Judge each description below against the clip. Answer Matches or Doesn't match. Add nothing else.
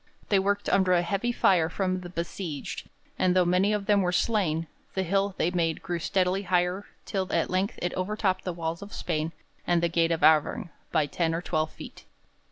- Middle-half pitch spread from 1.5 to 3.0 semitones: Matches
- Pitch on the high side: Doesn't match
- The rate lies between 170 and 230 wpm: Matches